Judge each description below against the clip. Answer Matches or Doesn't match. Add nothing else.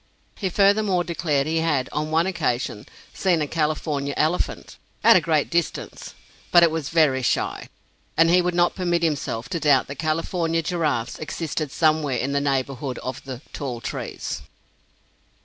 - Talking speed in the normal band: Matches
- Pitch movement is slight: Doesn't match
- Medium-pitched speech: Matches